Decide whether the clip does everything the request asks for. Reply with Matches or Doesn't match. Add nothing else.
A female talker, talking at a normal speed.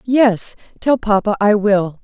Matches